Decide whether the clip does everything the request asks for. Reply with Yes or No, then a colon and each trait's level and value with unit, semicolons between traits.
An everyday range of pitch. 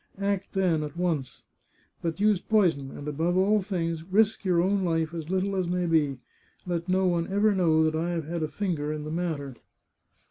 Yes: average, 3.1 semitones